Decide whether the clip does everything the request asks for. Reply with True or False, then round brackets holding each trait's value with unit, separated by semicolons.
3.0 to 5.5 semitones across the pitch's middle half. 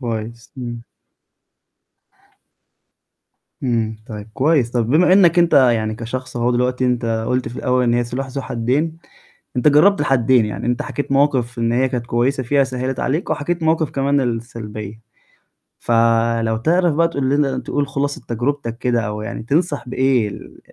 True (3.3 semitones)